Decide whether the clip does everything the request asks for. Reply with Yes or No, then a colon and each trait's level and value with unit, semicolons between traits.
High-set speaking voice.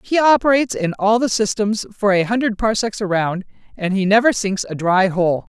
Yes: high, 210 Hz